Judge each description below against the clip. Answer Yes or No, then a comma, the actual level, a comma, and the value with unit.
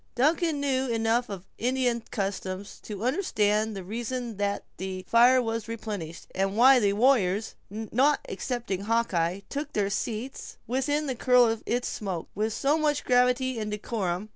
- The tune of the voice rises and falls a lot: No, average, 4.0 semitones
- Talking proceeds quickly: No, average, 155 wpm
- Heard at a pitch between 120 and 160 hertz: No, high, 230 Hz